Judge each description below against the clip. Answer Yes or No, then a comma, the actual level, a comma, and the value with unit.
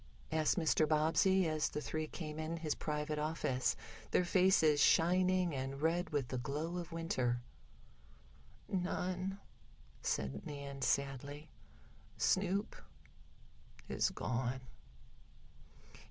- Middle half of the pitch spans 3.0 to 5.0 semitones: Yes, average, 3.9 semitones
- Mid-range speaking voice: Yes, medium, 155 Hz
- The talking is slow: Yes, slow, 105 wpm